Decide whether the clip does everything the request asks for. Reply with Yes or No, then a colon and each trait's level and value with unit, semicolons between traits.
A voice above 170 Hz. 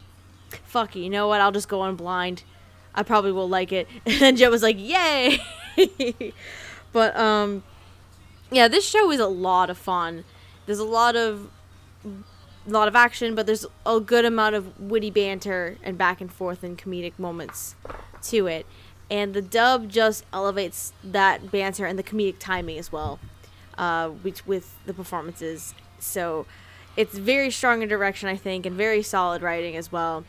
Yes: high, 190 Hz